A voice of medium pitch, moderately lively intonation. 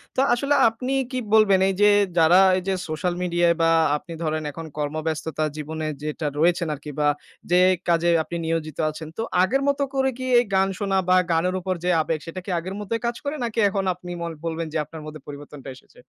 Yes: medium, 170 Hz; average, 3.8 semitones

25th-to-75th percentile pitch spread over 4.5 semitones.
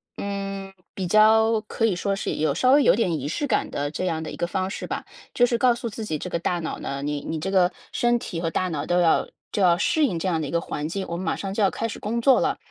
Yes: average, 4.9 semitones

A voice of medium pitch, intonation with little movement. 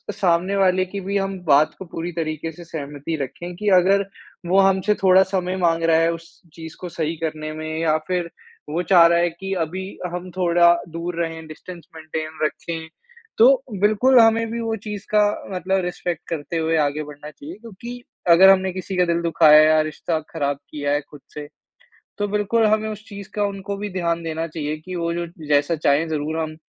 No: medium, 170 Hz; average, 3.4 semitones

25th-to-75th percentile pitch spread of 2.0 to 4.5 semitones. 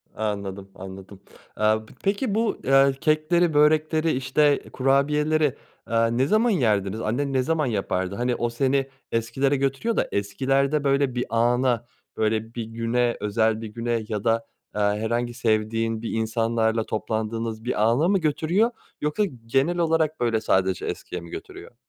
No: average, 4.9 semitones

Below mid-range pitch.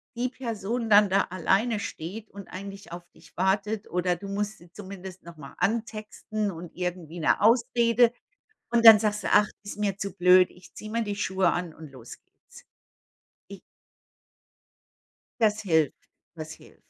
No: high, 200 Hz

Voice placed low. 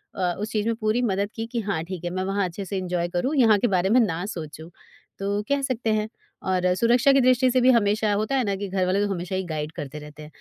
No: high, 200 Hz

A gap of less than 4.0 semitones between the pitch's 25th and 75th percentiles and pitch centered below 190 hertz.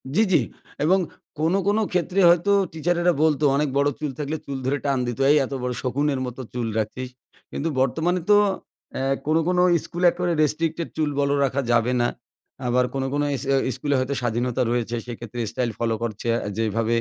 No: average, 4.7 semitones; medium, 140 Hz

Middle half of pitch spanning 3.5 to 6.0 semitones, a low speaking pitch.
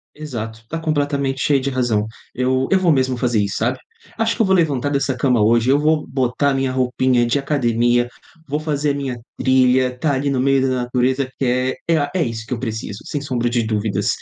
No: average, 2.8 semitones; low, 130 Hz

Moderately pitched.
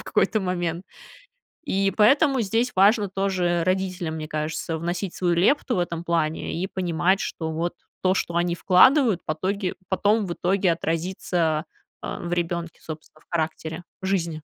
Yes: medium, 175 Hz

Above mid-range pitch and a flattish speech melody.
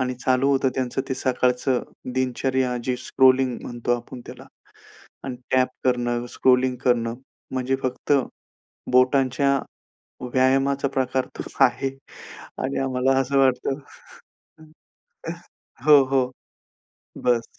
No: low, 130 Hz; narrow, 1.1 semitones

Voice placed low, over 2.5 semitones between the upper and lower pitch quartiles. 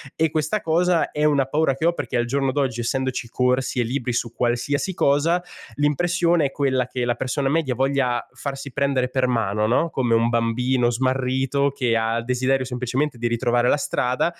Yes: low, 130 Hz; average, 2.9 semitones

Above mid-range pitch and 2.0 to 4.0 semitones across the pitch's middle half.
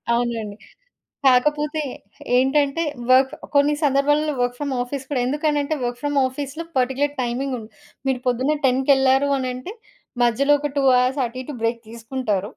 Yes: very high, 265 Hz; average, 2.7 semitones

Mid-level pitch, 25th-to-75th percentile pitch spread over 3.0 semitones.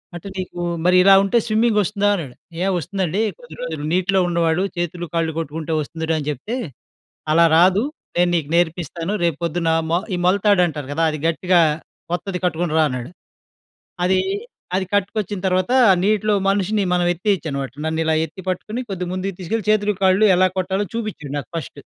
Yes: medium, 180 Hz; average, 3.4 semitones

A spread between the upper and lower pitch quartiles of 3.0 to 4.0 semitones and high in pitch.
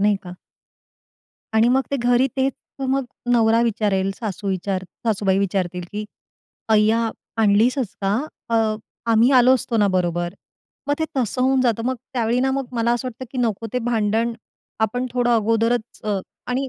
Yes: average, 3.4 semitones; high, 230 Hz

